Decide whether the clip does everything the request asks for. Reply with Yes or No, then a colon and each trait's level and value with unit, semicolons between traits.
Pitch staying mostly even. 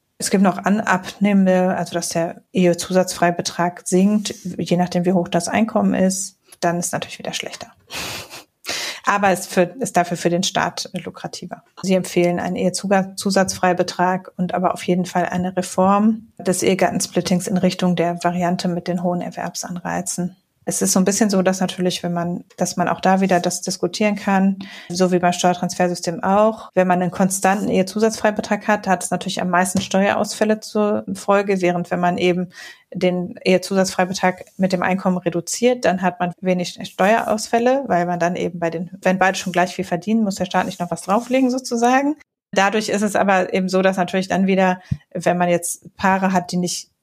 Yes: narrow, 2.0 semitones